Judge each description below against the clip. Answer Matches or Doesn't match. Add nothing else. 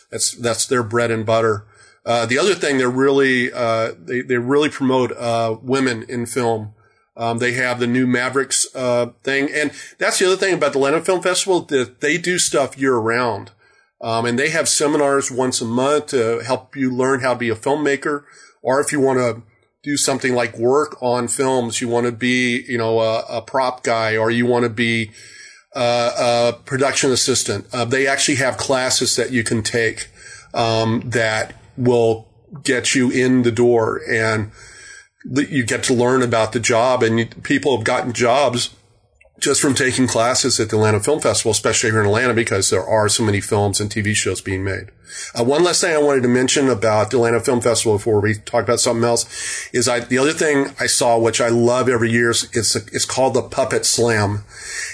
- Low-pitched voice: Matches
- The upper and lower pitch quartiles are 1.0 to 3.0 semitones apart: Matches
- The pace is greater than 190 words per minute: Matches